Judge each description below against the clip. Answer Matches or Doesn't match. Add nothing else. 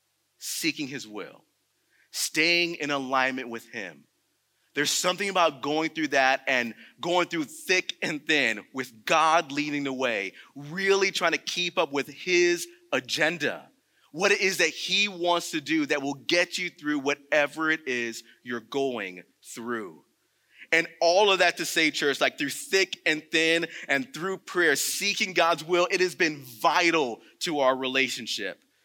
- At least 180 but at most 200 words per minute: Doesn't match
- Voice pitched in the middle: Matches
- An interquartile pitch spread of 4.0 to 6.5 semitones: Matches